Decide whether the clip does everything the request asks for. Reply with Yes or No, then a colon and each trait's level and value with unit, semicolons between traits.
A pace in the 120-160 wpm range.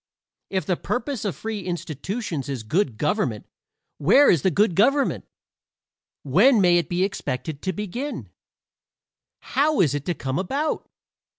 Yes: average, 140 wpm